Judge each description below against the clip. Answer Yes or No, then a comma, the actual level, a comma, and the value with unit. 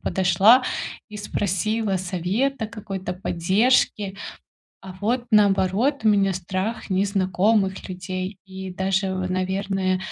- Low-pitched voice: No, high, 190 Hz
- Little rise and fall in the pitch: Yes, narrow, 2.1 semitones